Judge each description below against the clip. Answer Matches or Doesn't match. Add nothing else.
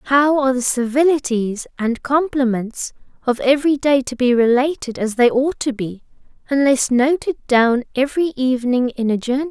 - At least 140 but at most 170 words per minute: Matches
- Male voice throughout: Doesn't match